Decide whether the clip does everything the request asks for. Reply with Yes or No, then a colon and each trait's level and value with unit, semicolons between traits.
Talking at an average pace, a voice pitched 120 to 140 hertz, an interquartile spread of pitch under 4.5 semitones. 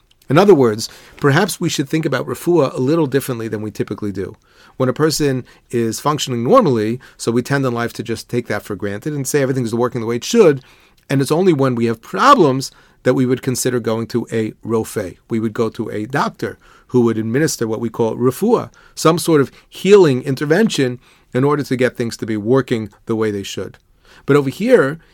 No: fast, 215 wpm; low, 125 Hz; average, 3.5 semitones